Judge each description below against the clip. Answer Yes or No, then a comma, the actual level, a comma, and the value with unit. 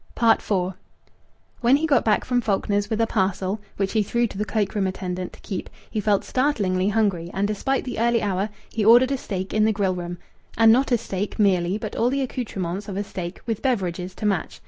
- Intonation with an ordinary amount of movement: Yes, average, 3.4 semitones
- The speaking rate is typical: No, fast, 215 wpm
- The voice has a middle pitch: No, high, 205 Hz